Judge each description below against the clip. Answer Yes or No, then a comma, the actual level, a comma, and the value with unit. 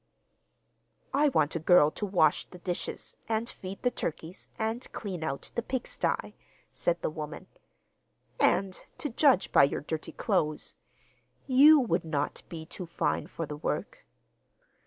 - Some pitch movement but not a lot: No, wide, 6.4 semitones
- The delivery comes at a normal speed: Yes, average, 155 wpm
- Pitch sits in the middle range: Yes, medium, 180 Hz